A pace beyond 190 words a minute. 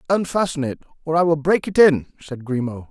Yes: fast, 205 wpm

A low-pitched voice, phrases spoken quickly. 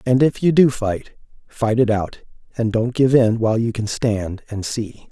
Yes: low, 115 Hz; fast, 210 wpm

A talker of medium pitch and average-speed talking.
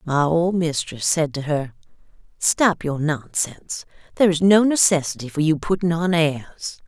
Yes: medium, 160 Hz; average, 155 wpm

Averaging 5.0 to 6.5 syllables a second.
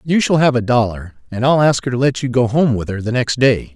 Yes: 5.7 syllables/s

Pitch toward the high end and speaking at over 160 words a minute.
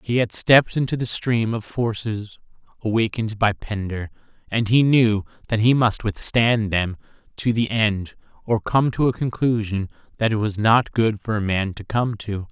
No: low, 110 Hz; average, 180 wpm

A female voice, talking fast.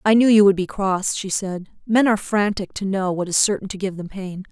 Yes: female; fast, 265 wpm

